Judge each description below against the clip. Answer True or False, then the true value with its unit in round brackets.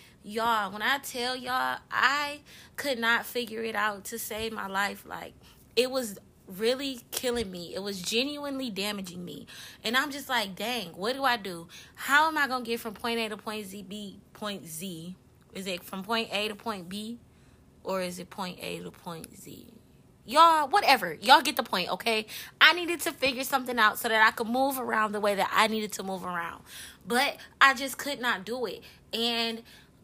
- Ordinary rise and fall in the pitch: True (4.2 semitones)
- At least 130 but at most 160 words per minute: False (200 wpm)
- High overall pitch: True (225 Hz)